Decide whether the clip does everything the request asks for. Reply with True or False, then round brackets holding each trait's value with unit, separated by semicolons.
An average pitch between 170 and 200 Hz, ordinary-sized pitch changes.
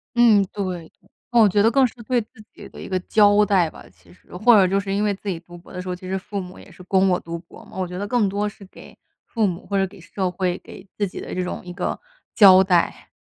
False (190 Hz; 2.3 semitones)